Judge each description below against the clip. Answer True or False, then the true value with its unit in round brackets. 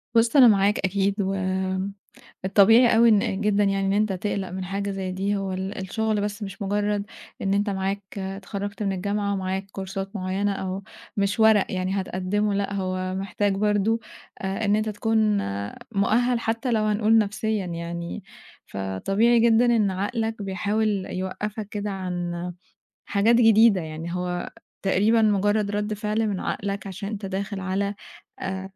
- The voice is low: False (200 Hz)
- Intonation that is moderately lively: False (1.8 semitones)